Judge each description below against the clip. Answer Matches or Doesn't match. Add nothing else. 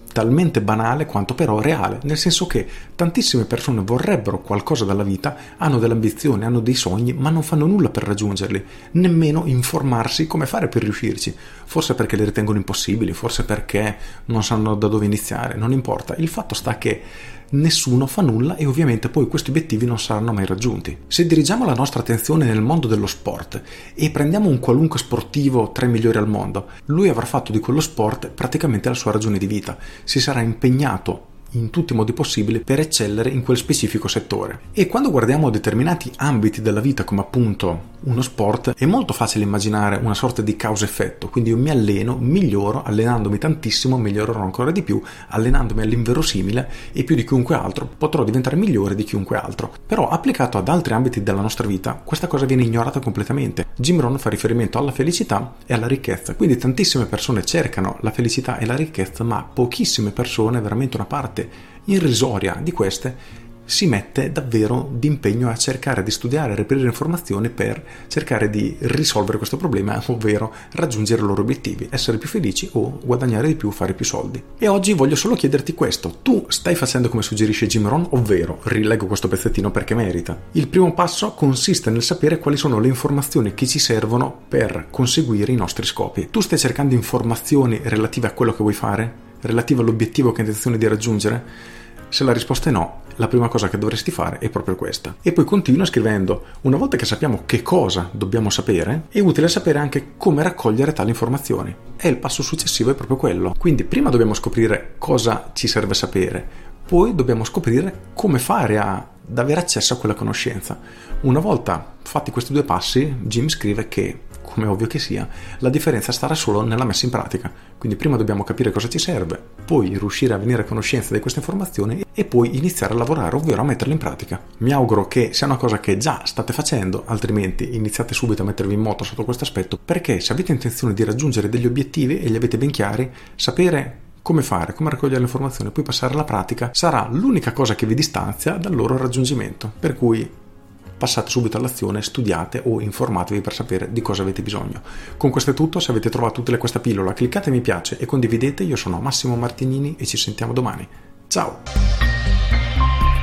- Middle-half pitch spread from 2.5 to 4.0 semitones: Doesn't match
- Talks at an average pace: Doesn't match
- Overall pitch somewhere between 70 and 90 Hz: Doesn't match